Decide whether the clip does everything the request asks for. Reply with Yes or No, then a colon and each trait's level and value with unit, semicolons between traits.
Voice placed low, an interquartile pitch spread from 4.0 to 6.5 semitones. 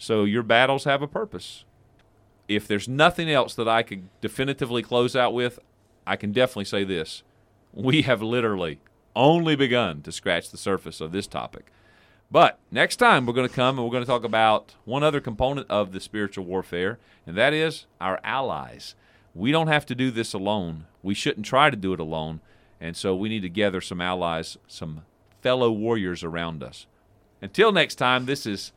Yes: low, 110 Hz; average, 4.7 semitones